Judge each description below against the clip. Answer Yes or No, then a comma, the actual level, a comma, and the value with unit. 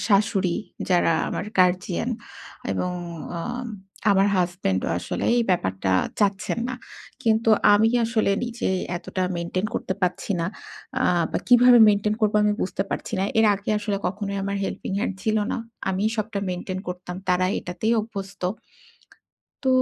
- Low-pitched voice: No, high, 200 Hz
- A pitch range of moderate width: Yes, average, 3.2 semitones